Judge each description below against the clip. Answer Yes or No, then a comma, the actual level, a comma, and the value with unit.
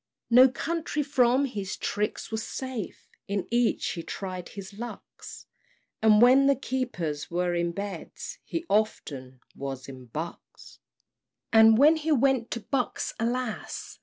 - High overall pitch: Yes, high, 220 Hz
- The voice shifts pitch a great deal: Yes, wide, 6.3 semitones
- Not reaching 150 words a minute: Yes, slow, 135 wpm